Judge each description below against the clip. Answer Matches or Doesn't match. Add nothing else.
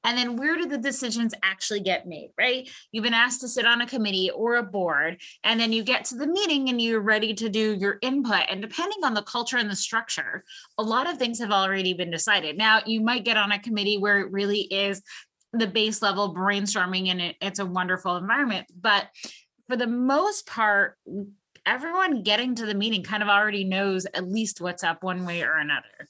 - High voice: Matches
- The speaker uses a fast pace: Matches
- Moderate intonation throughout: Matches